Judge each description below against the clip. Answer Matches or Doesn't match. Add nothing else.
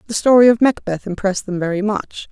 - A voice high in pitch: Matches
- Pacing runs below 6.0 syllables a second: Doesn't match